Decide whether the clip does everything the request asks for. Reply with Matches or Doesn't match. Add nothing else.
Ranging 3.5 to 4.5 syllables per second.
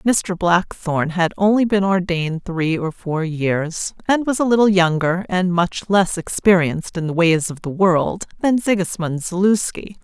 Matches